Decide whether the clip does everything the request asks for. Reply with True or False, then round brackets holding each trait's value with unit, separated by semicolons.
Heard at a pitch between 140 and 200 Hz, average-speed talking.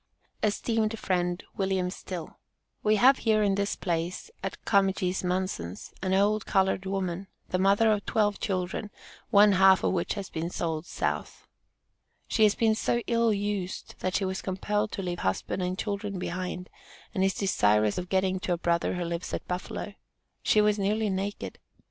True (190 Hz; 170 wpm)